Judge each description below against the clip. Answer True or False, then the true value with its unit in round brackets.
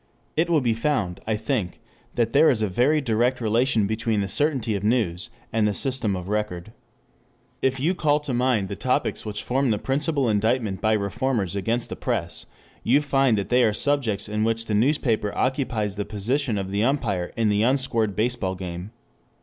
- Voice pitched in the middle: False (115 Hz)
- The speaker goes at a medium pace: True (185 wpm)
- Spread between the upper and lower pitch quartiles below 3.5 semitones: False (4.2 semitones)